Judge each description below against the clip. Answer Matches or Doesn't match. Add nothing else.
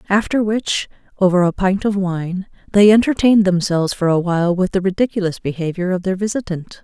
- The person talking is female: Matches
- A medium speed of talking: Matches